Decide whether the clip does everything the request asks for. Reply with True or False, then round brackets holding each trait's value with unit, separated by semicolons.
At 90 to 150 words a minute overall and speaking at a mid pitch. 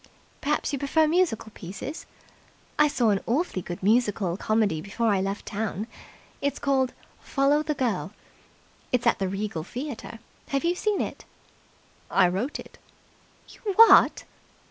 False (145 wpm; 235 Hz)